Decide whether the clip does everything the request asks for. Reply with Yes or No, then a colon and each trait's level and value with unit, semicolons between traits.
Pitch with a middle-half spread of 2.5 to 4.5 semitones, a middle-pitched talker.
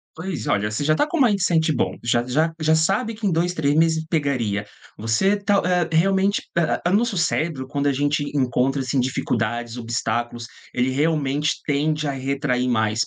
No: average, 5.2 semitones; medium, 145 Hz